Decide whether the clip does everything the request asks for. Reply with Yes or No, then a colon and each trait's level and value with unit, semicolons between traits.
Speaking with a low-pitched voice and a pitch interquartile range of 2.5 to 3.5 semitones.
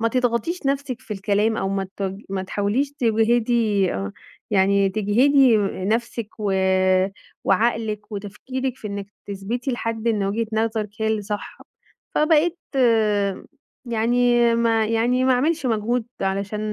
No: high, 225 Hz; average, 3.1 semitones